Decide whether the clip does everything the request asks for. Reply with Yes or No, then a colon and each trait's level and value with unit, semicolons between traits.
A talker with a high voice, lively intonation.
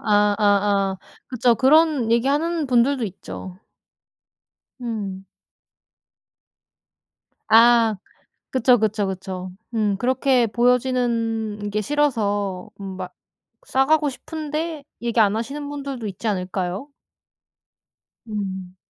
No: high, 225 Hz; average, 4.6 semitones